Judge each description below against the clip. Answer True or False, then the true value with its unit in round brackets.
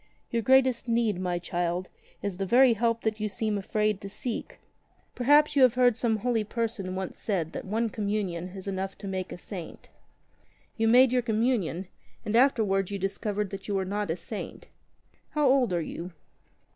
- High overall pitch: True (210 Hz)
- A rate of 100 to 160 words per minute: False (185 wpm)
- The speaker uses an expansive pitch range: False (3.7 semitones)